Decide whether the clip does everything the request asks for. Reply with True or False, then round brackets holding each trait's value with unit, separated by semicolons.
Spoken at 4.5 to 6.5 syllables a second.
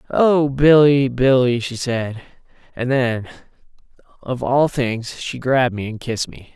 False (4.1 syllables/s)